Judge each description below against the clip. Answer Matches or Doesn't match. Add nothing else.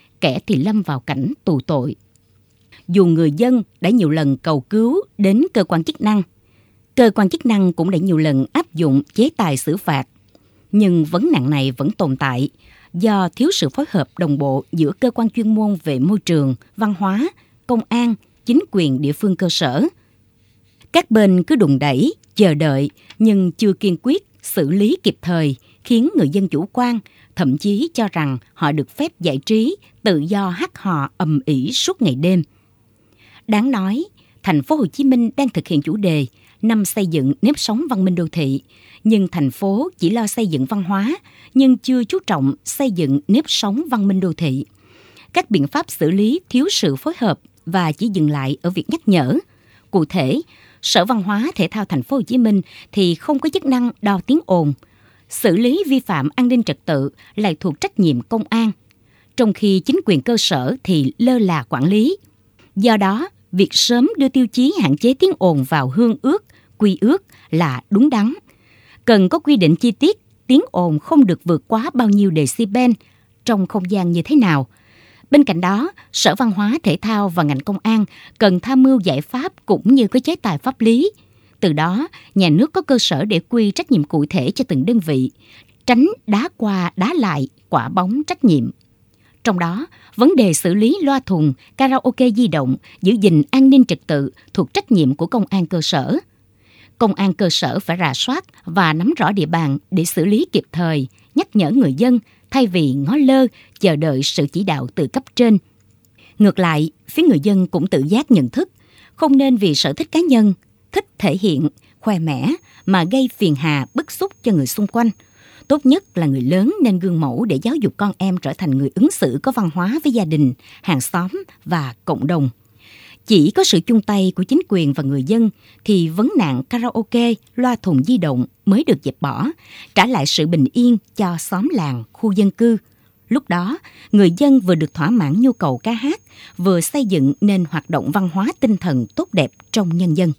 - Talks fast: Doesn't match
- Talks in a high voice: Matches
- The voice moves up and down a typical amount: Doesn't match